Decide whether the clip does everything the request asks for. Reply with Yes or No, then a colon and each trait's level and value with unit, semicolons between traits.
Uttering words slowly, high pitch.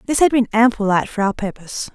No: fast, 245 wpm; high, 220 Hz